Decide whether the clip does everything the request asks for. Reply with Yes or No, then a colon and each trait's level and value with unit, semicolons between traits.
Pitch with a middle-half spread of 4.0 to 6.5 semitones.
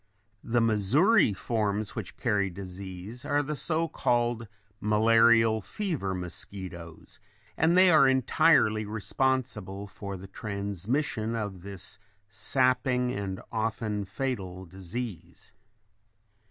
Yes: average, 4.5 semitones